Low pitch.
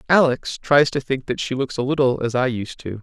Yes: low, 130 Hz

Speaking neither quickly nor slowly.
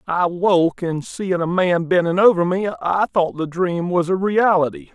Yes: average, 195 wpm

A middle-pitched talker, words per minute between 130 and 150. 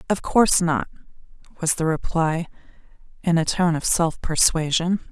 Yes: medium, 170 Hz; average, 140 wpm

